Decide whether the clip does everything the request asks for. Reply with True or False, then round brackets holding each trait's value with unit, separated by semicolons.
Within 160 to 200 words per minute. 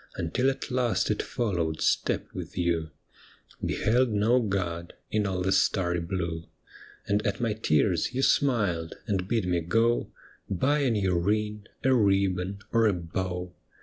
False (150 wpm)